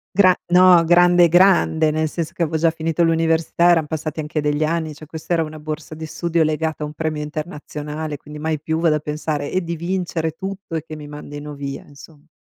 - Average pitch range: No, narrow, 1.9 semitones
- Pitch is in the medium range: Yes, medium, 160 Hz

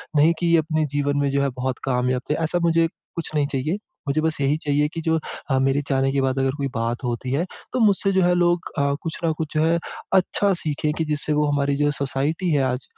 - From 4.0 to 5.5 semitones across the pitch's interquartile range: No, average, 3.2 semitones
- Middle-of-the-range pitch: Yes, medium, 145 Hz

